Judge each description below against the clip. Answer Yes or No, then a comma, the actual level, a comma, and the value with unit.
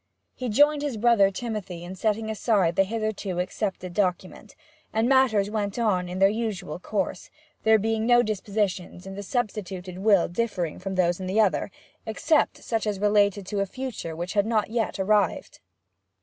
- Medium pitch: No, high, 205 Hz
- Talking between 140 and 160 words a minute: No, average, 170 wpm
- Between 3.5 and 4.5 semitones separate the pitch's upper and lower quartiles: No, average, 2.9 semitones